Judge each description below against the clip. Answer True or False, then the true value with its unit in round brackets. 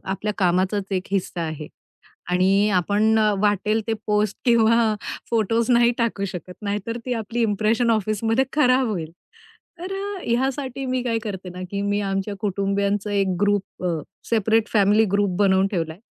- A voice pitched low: False (210 Hz)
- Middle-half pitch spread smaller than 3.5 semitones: True (2.9 semitones)